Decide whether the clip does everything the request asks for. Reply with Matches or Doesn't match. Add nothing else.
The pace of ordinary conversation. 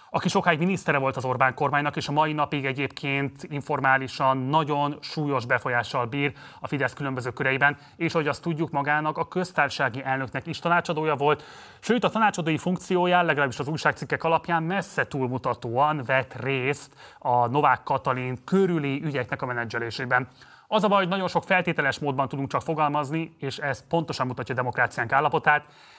Doesn't match